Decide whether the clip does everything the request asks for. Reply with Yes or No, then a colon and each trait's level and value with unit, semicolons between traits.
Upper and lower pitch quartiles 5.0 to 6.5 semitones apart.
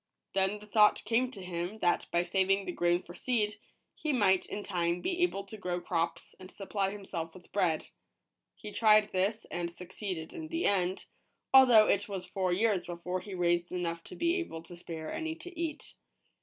No: average, 3.4 semitones